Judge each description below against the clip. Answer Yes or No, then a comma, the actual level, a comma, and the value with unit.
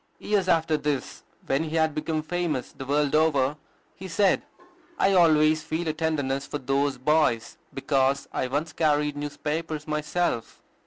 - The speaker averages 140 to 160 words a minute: Yes, average, 150 wpm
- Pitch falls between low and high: Yes, medium, 150 Hz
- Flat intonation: Yes, narrow, 2.3 semitones